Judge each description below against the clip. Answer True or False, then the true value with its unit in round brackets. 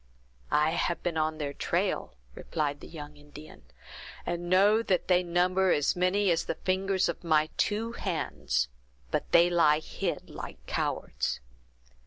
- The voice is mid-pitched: True (175 Hz)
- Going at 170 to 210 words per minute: False (150 wpm)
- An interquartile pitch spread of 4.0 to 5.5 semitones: False (3.2 semitones)